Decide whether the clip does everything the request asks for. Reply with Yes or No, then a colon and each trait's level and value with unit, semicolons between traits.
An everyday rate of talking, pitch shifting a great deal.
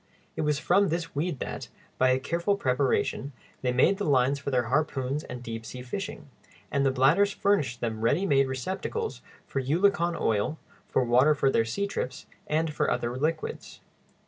No: average, 170 wpm; average, 5.0 semitones